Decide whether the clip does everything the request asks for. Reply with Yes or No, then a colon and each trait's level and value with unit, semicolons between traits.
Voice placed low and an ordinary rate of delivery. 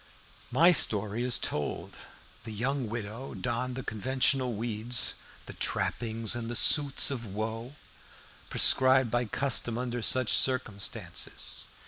No: low, 120 Hz; slow, 120 wpm